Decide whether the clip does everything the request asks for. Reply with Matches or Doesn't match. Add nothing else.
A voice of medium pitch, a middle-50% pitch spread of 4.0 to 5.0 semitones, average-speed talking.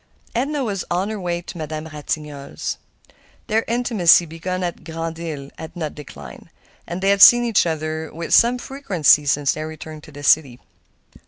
Matches